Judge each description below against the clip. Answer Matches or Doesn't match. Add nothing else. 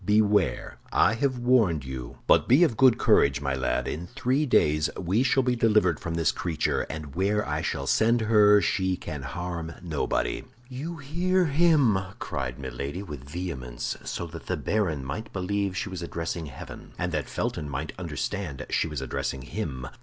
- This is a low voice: Matches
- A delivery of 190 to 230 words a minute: Doesn't match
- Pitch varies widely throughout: Matches